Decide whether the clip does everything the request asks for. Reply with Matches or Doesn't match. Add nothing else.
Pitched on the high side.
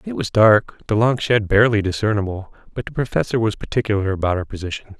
Doesn't match